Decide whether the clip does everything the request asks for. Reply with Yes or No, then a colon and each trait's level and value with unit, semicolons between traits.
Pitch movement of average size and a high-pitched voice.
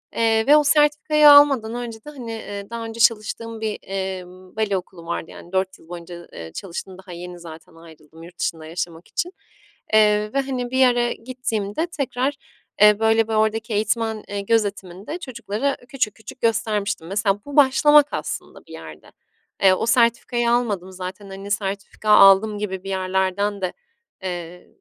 Yes: average, 3.8 semitones; high, 210 Hz